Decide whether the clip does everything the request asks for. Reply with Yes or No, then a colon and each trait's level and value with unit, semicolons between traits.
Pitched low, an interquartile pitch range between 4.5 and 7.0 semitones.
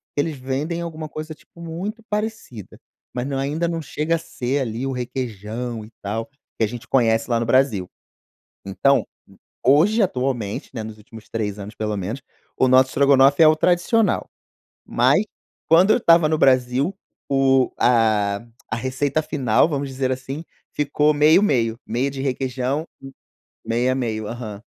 Yes: low, 130 Hz; average, 5.0 semitones